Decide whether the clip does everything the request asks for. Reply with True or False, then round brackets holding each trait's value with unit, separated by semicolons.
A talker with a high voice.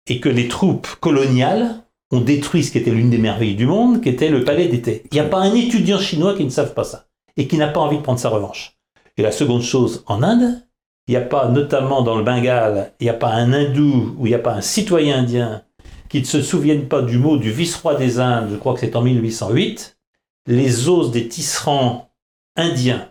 False (130 Hz)